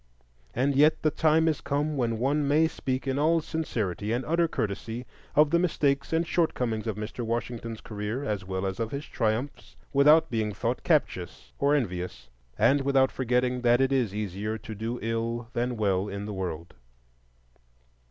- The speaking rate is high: No, average, 170 wpm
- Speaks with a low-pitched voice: Yes, low, 120 Hz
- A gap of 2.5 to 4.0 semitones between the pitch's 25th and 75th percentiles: No, average, 4.9 semitones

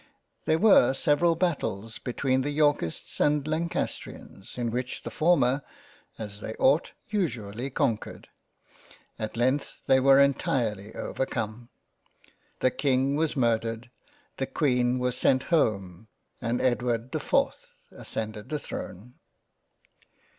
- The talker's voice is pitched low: Yes, low, 125 Hz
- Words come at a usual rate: No, slow, 125 wpm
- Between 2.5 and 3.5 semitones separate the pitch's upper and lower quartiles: No, average, 4.3 semitones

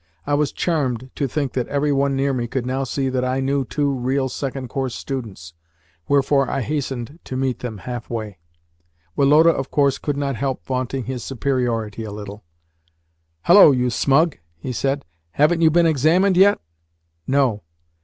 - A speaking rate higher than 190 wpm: No, average, 170 wpm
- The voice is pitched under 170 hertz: Yes, low, 135 Hz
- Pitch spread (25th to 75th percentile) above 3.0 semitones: No, narrow, 2.4 semitones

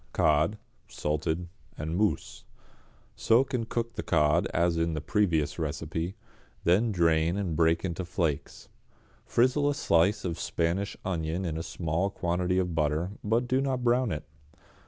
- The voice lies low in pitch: Yes, very low, 85 Hz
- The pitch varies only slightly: No, average, 4.4 semitones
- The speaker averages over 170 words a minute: No, average, 155 wpm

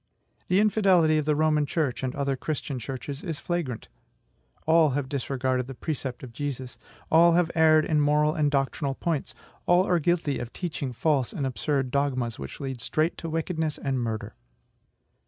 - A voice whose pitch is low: No, medium, 145 Hz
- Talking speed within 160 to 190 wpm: Yes, average, 170 wpm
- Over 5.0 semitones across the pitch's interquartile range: No, average, 3.4 semitones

